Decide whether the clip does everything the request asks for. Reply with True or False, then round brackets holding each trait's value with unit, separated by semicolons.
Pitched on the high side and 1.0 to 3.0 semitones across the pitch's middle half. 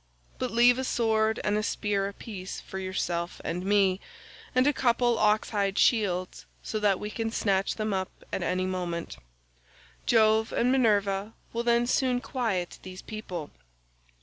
False (210 Hz; 3.5 semitones)